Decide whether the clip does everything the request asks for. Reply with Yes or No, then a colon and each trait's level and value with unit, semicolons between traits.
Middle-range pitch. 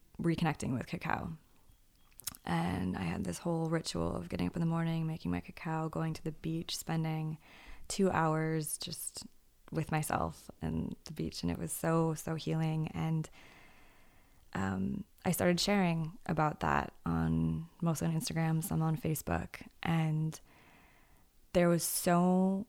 Yes: medium, 160 Hz